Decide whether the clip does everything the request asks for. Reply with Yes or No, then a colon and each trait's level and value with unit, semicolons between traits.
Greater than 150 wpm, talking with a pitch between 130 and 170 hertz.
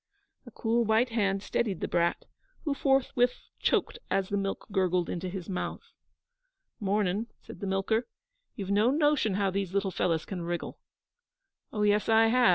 No: average, 165 wpm; high, 200 Hz